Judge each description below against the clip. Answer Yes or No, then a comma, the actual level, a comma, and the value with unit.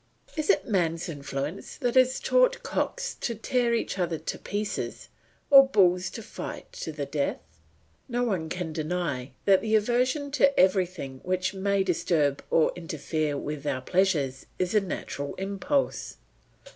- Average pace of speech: Yes, average, 150 wpm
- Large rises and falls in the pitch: Yes, wide, 6.6 semitones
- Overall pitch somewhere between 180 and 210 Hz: Yes, medium, 185 Hz